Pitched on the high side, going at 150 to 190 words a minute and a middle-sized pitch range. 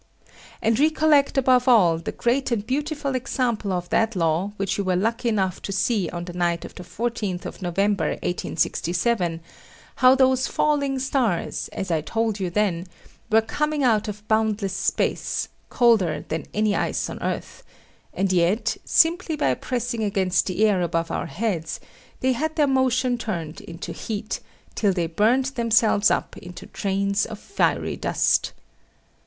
No: high, 215 Hz; average, 160 wpm; wide, 5.7 semitones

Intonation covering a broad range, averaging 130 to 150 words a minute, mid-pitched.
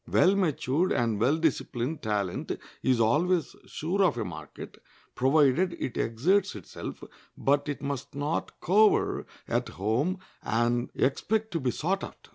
Yes: wide, 6.9 semitones; average, 140 wpm; medium, 145 Hz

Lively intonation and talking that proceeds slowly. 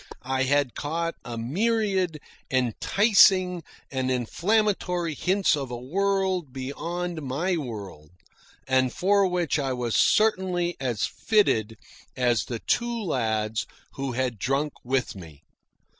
Yes: wide, 6.8 semitones; slow, 120 wpm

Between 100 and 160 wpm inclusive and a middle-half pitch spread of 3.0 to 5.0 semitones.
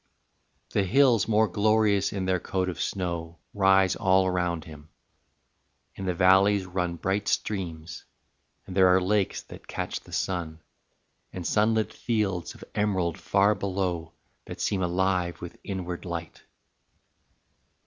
No: average, 140 wpm; narrow, 2.4 semitones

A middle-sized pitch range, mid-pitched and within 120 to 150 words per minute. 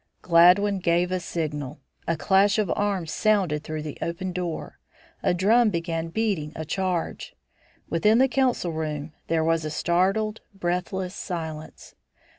Yes: average, 3.5 semitones; medium, 175 Hz; average, 140 wpm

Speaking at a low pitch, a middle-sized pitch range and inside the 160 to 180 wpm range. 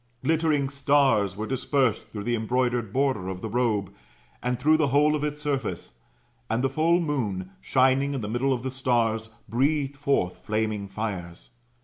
Yes: low, 125 Hz; average, 4.4 semitones; average, 165 wpm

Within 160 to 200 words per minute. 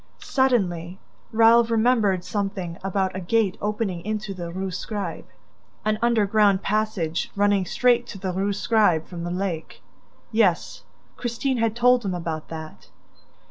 No: average, 140 wpm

